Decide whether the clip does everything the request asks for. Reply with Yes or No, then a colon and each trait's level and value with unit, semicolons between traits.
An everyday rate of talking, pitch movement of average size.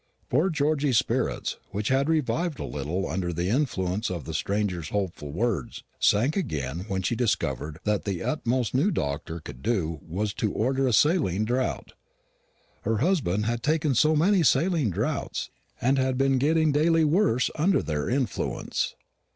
No: average, 160 wpm; wide, 8.2 semitones